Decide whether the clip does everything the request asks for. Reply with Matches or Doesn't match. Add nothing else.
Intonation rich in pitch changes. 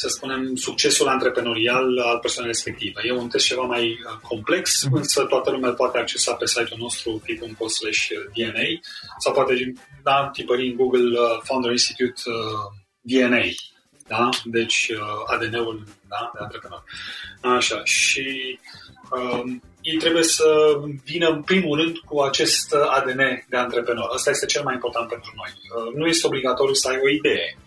Doesn't match